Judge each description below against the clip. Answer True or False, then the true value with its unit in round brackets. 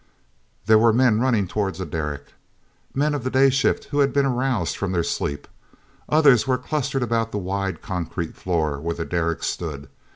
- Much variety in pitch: True (7.5 semitones)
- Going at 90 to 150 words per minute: False (175 wpm)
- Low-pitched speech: True (105 Hz)